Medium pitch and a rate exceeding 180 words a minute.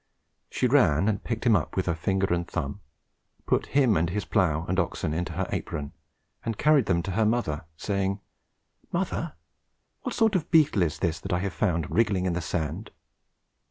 No: very low, 95 Hz; average, 190 wpm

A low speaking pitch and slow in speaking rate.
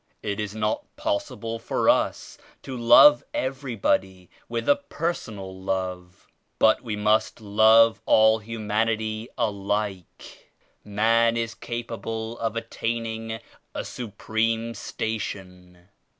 Yes: low, 110 Hz; slow, 105 wpm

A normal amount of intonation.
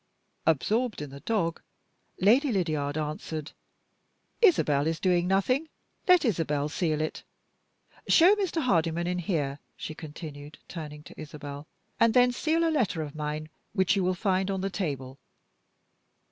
No: wide, 6.2 semitones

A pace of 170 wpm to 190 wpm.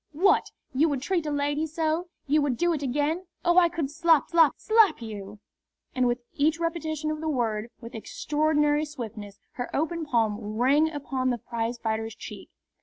Yes: average, 175 wpm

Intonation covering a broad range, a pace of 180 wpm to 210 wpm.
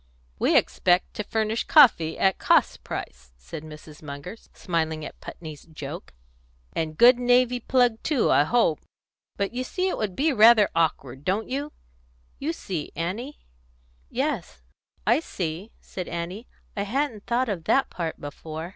No: wide, 7.5 semitones; average, 150 wpm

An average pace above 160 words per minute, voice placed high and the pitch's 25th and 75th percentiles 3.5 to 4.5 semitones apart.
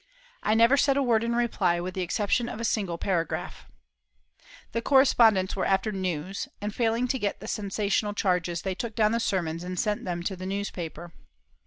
Yes: average, 190 wpm; high, 200 Hz; average, 4.0 semitones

